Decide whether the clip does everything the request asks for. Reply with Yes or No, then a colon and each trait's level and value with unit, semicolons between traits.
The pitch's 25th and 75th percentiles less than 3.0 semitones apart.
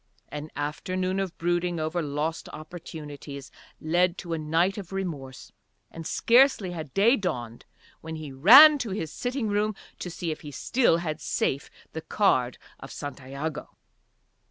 No: average, 4.4 semitones